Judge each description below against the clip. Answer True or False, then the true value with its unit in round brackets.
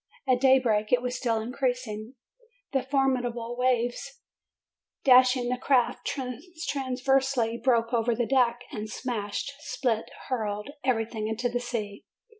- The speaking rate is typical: False (125 wpm)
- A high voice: True (245 Hz)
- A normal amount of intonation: False (2.2 semitones)